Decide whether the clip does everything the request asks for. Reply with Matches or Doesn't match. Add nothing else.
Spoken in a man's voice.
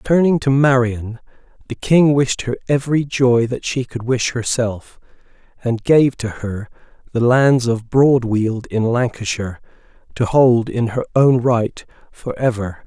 Matches